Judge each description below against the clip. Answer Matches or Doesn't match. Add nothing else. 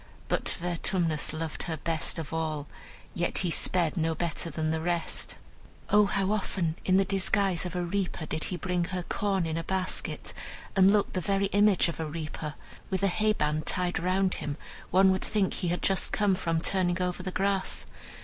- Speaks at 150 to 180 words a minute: Doesn't match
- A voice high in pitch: Doesn't match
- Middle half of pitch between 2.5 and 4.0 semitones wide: Matches